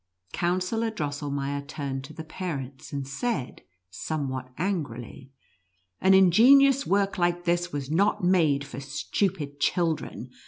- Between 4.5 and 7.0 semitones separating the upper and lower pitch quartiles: Yes, average, 5.0 semitones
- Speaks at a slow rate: Yes, slow, 130 wpm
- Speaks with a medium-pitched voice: Yes, medium, 155 Hz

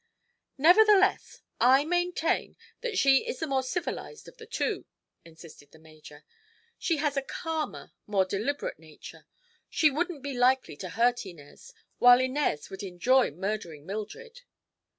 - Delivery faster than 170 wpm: No, average, 140 wpm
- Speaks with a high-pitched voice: Yes, very high, 260 Hz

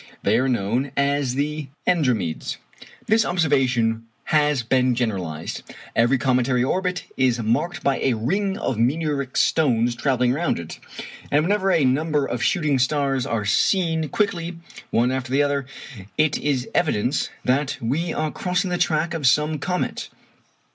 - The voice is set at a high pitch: No, medium, 140 Hz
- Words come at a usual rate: Yes, average, 150 wpm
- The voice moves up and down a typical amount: Yes, average, 4.6 semitones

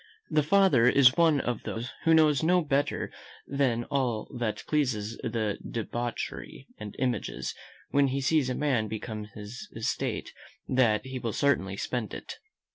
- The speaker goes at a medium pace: Yes, average, 150 wpm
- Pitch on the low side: Yes, low, 125 Hz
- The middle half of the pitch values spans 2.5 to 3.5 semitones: No, average, 4.2 semitones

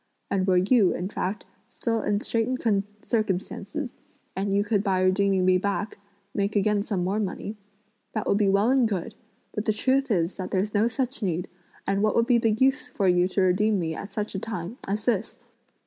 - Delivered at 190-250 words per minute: Yes, average, 200 wpm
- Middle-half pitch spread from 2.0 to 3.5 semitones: Yes, average, 2.7 semitones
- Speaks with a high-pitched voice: Yes, high, 205 Hz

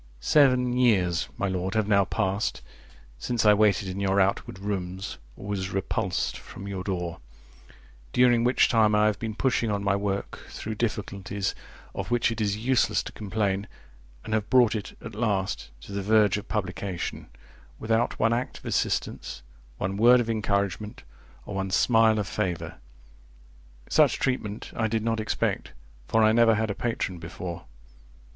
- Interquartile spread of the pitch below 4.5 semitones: Yes, average, 2.7 semitones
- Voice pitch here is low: Yes, low, 105 Hz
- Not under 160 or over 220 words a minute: Yes, average, 165 wpm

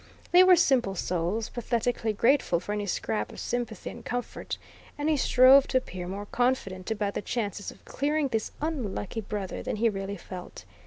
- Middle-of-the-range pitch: No, high, 220 Hz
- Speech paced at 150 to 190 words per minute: Yes, average, 175 wpm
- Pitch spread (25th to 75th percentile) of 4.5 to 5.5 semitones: Yes, average, 4.8 semitones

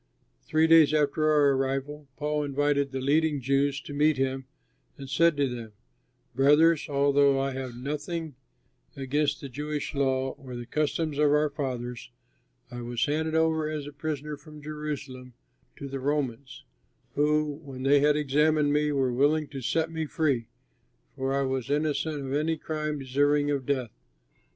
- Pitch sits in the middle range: Yes, medium, 145 Hz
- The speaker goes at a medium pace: Yes, average, 165 wpm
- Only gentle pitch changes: Yes, narrow, 2.1 semitones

